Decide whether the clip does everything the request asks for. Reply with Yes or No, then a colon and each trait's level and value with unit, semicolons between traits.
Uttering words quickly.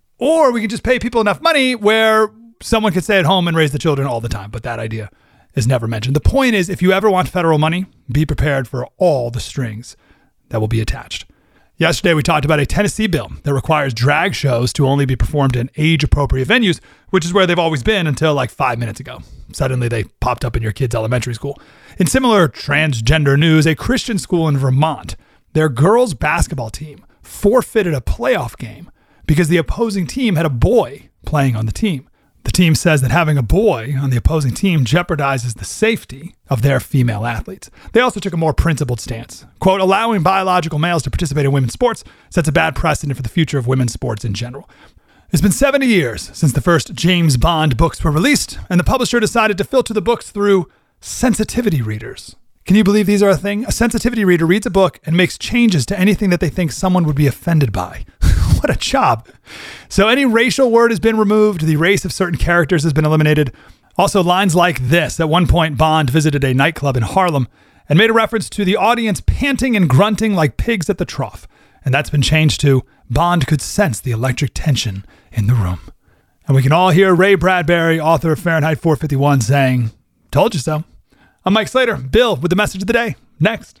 Yes: fast, 210 wpm